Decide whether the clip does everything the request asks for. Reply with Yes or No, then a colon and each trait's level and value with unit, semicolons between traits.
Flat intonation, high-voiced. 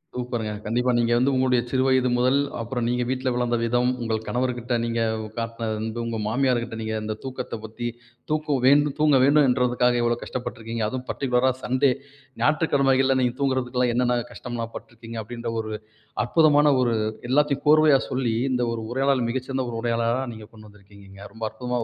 No: narrow, 2.2 semitones; low, 125 Hz